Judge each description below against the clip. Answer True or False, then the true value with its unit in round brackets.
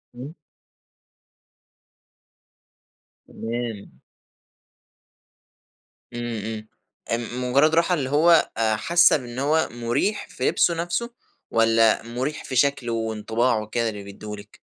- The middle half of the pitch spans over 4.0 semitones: True (4.5 semitones)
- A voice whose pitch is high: False (120 Hz)